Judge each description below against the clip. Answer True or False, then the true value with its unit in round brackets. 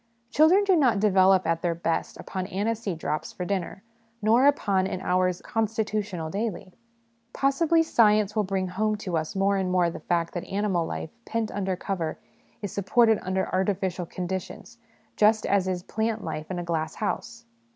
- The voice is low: False (195 Hz)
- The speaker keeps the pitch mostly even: False (3.2 semitones)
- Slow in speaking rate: False (175 wpm)